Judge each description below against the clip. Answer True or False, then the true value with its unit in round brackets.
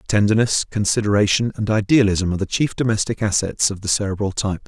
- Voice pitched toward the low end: True (105 Hz)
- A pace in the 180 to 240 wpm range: False (165 wpm)